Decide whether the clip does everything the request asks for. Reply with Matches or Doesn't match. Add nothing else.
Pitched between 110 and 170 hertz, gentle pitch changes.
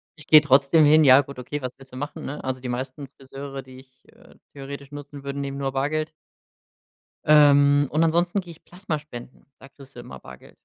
Matches